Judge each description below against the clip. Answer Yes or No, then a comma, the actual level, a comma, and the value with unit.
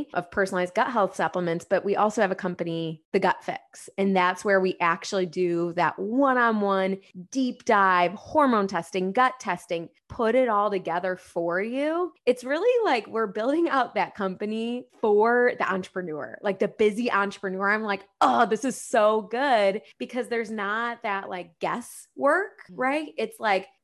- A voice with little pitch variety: No, average, 4.7 semitones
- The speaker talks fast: No, average, 170 wpm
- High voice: Yes, high, 200 Hz